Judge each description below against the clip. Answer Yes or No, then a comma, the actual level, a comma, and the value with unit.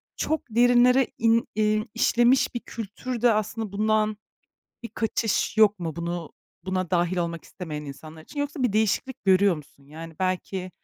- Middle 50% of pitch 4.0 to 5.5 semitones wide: Yes, average, 5.0 semitones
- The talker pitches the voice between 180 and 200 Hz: No, high, 210 Hz